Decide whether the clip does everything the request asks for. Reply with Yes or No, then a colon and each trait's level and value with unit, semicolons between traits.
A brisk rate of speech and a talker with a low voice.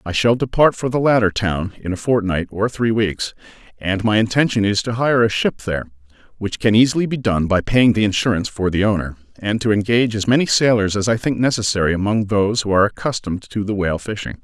Yes: fast, 220 wpm; low, 105 Hz